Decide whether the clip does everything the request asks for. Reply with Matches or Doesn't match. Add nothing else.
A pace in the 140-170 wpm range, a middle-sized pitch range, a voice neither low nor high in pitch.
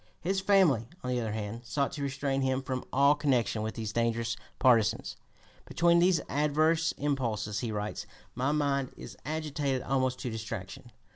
Doesn't match